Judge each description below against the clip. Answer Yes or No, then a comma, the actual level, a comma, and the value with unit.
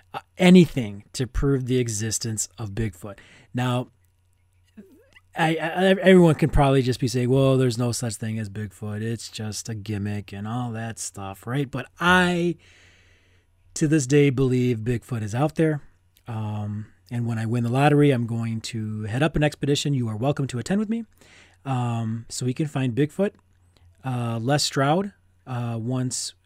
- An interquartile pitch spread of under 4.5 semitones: No, average, 5.1 semitones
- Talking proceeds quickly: No, average, 170 wpm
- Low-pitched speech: Yes, low, 120 Hz